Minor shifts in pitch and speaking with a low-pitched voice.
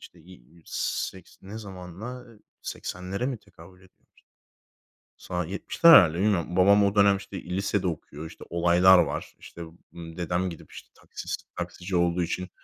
Yes: narrow, 2.3 semitones; very low, 90 Hz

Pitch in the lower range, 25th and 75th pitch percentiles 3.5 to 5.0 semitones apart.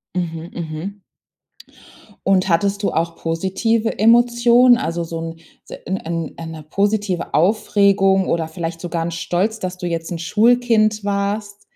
No: high, 190 Hz; average, 4.0 semitones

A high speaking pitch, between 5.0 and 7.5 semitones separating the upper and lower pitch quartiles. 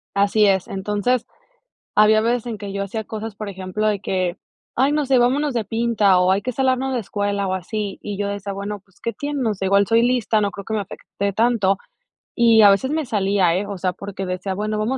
No: high, 205 Hz; average, 2.8 semitones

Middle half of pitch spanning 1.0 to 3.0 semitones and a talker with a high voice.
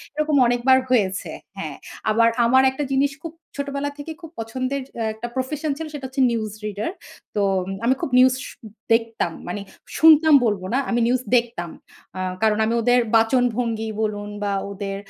No: average, 4.1 semitones; high, 245 Hz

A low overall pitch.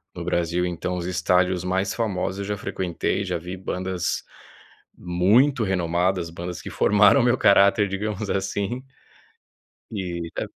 Yes: very low, 95 Hz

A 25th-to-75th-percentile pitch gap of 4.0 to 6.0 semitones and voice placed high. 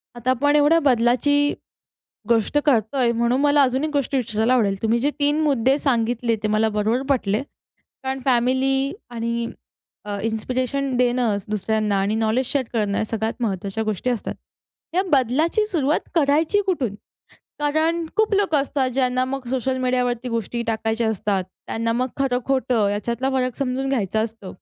No: average, 3.6 semitones; very high, 250 Hz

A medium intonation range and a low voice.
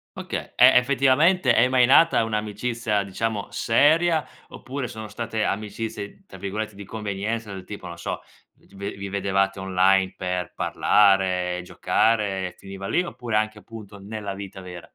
Yes: average, 3.0 semitones; low, 105 Hz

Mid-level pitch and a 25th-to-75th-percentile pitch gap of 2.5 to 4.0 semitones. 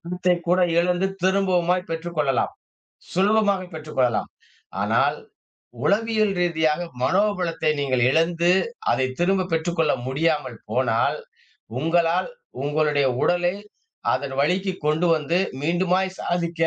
Yes: medium, 170 Hz; average, 3.2 semitones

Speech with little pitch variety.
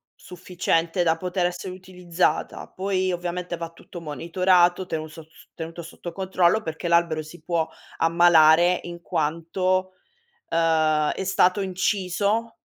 Yes: narrow, 1.9 semitones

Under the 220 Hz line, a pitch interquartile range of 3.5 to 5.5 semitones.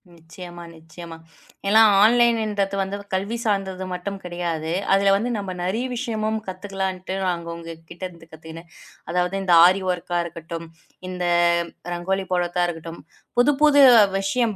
No: medium, 185 Hz; average, 3.0 semitones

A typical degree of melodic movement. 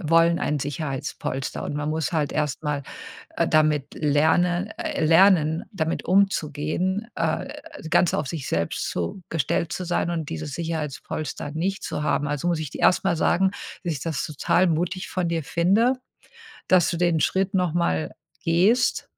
Yes: average, 3.0 semitones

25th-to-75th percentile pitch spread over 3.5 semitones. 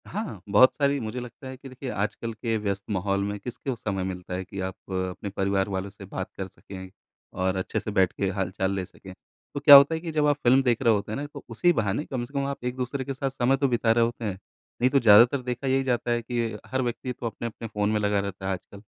Yes: average, 4.9 semitones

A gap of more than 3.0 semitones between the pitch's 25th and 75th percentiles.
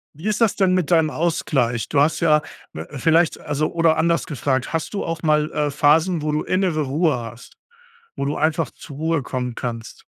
No: average, 2.7 semitones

